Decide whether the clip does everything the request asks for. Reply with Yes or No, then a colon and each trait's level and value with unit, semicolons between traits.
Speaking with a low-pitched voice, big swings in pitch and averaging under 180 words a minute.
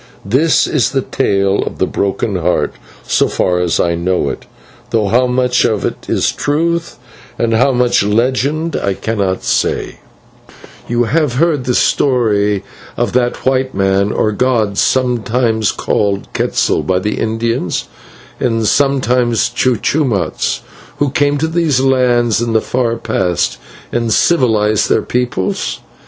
No: low, 120 Hz; average, 3.8 semitones; average, 145 wpm